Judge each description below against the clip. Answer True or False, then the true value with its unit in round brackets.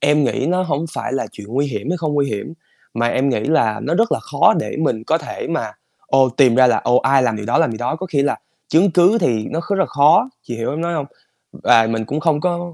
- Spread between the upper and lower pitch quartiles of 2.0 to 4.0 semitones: False (5.6 semitones)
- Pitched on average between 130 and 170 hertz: True (140 Hz)